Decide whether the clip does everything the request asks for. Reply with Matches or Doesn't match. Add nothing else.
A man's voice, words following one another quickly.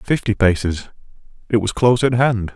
Doesn't match